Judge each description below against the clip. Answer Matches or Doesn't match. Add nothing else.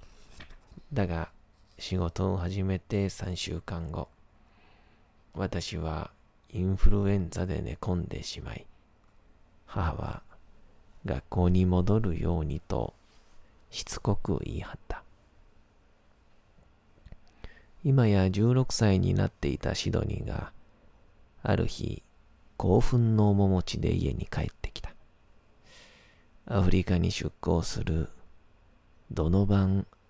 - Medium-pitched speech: Doesn't match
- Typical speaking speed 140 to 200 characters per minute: Matches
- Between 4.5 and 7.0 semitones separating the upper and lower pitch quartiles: Doesn't match